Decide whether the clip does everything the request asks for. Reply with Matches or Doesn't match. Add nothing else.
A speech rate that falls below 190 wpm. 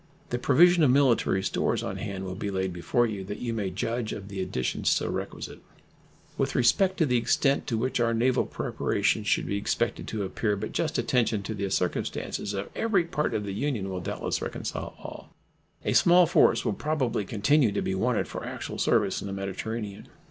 Doesn't match